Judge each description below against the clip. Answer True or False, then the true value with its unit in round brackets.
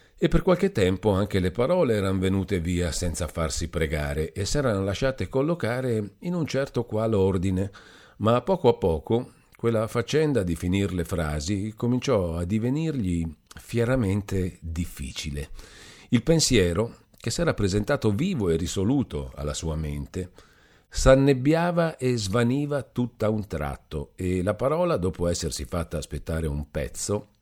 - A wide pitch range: True (6.1 semitones)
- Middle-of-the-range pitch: False (100 Hz)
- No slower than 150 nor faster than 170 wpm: False (140 wpm)